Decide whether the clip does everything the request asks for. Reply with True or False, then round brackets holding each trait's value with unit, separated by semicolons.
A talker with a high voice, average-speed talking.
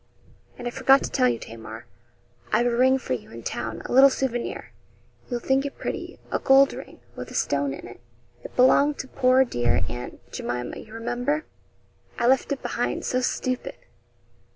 True (245 Hz; 180 wpm)